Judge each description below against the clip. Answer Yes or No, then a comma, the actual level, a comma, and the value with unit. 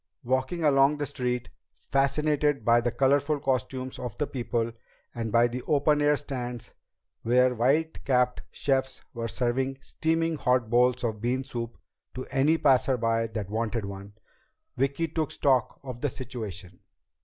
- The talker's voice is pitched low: Yes, low, 130 Hz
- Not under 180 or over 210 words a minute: No, average, 150 wpm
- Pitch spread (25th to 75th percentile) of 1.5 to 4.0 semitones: Yes, average, 3.0 semitones